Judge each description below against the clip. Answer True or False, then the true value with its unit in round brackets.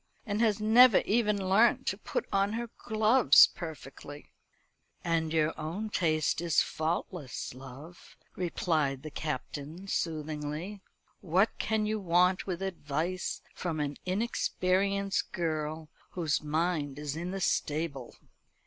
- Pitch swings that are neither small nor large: True (4.4 semitones)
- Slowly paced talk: True (120 wpm)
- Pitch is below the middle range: False (170 Hz)